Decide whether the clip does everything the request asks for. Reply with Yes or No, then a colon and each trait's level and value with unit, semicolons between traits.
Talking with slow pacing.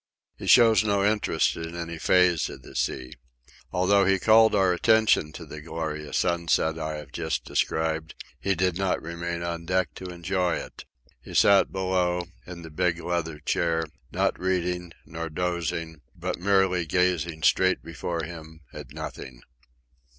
No: average, 155 wpm